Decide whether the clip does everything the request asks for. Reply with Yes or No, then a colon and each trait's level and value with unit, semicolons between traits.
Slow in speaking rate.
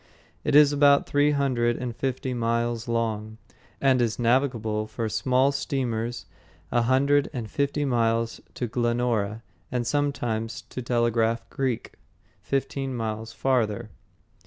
Yes: slow, 125 wpm